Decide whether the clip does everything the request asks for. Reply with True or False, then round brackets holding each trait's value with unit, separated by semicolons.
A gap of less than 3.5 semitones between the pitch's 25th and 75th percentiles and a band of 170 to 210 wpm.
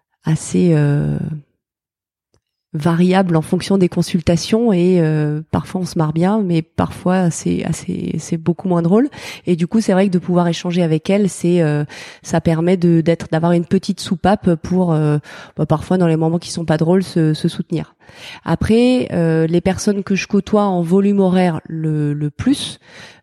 True (2.7 semitones; 180 wpm)